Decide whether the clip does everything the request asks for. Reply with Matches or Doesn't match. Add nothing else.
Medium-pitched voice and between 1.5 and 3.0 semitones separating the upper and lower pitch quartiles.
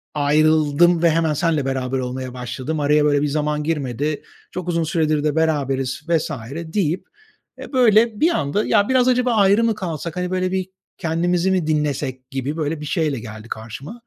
Doesn't match